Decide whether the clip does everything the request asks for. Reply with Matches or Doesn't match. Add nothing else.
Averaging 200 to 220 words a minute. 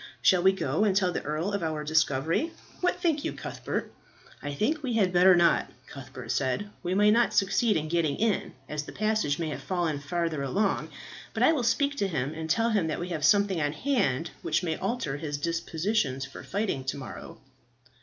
Matches